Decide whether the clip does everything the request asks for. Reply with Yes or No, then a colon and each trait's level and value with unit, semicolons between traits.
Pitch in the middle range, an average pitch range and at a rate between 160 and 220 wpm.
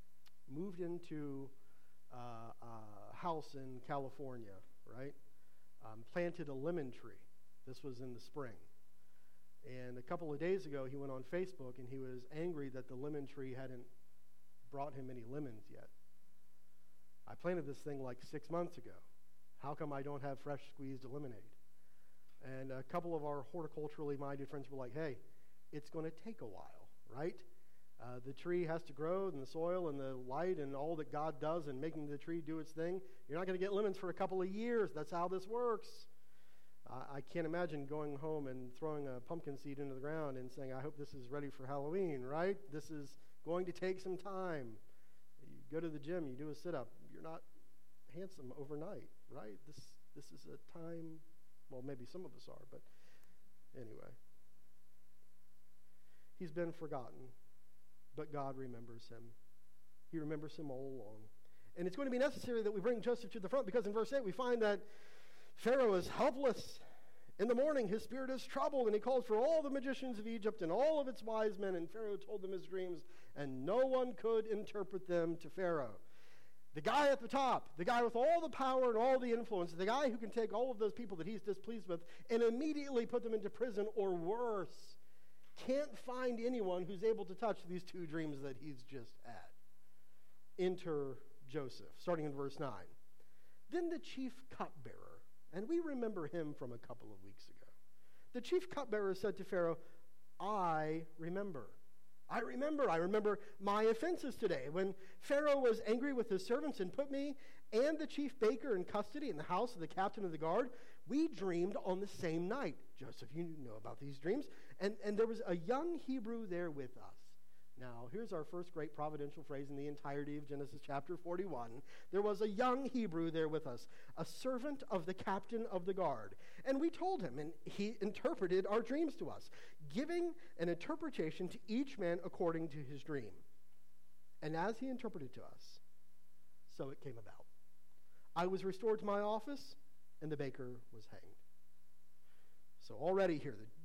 No: medium, 160 Hz; wide, 8.2 semitones; average, 190 wpm